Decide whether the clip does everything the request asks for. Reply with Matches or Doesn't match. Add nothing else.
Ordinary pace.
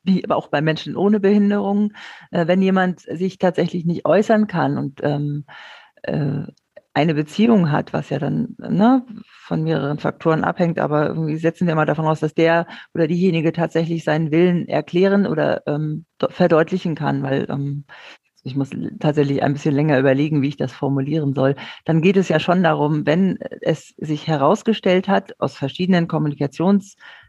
Matches